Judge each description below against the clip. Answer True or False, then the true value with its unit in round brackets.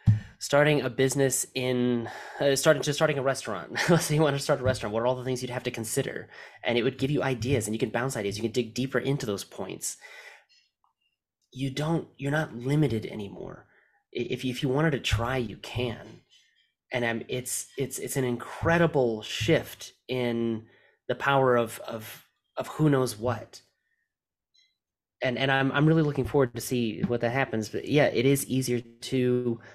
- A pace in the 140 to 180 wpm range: False (190 wpm)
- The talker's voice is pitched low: True (130 Hz)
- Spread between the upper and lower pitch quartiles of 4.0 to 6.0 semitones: False (2.8 semitones)